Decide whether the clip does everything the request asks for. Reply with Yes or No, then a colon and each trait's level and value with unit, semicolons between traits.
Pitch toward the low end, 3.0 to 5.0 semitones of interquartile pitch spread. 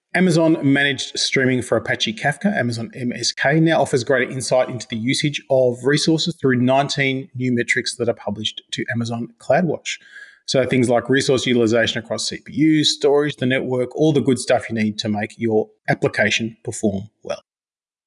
Yes: low, 130 Hz; average, 3.3 semitones